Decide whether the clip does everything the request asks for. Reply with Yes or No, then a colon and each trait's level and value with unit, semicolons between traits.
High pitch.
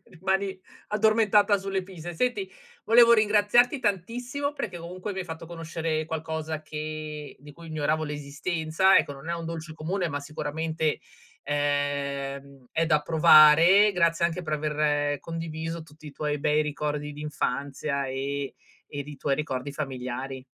No: medium, 155 Hz